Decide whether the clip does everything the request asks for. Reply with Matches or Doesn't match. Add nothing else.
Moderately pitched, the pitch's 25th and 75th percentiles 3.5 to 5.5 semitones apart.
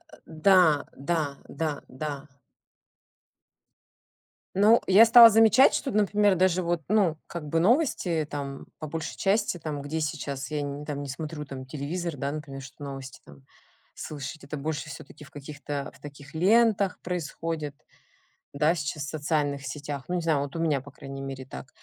Matches